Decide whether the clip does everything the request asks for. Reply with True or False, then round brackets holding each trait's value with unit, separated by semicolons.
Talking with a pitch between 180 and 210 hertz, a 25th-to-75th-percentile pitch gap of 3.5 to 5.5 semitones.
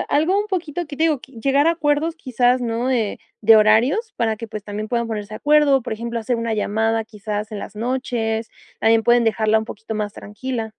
False (230 Hz; 3.8 semitones)